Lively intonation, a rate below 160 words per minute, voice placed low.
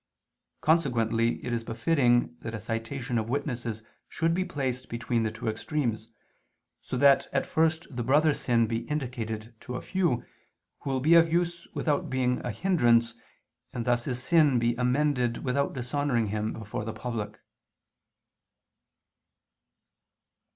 No: average, 3.9 semitones; average, 145 wpm; low, 125 Hz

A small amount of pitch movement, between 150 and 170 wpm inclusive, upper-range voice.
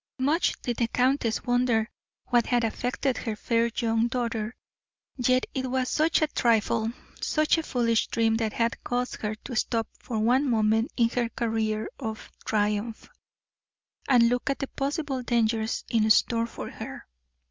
Yes: narrow, 2.2 semitones; average, 160 wpm; high, 235 Hz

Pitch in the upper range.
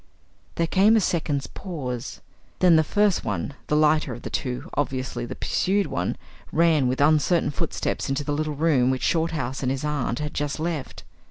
No: medium, 150 Hz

